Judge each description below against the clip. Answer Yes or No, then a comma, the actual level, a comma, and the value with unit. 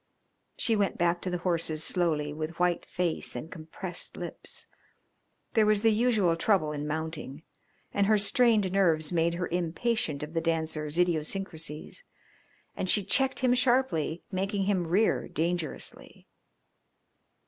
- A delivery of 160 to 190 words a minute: No, slow, 135 wpm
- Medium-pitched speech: Yes, medium, 175 Hz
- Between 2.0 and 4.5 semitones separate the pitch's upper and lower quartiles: Yes, average, 4.2 semitones